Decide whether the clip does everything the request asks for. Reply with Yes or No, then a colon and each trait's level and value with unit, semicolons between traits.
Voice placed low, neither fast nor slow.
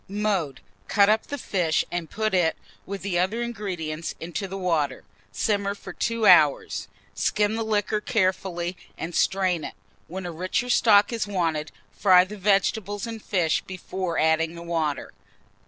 No: high, 190 Hz; average, 155 wpm